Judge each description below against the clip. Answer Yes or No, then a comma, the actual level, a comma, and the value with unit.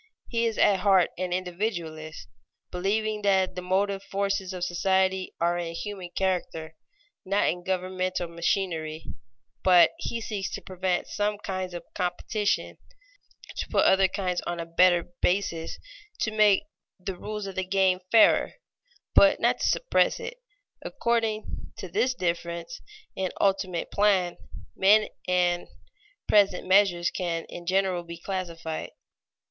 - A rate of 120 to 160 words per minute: Yes, slow, 135 wpm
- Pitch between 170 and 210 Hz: Yes, medium, 185 Hz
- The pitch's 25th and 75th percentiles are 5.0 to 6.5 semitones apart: No, narrow, 2.4 semitones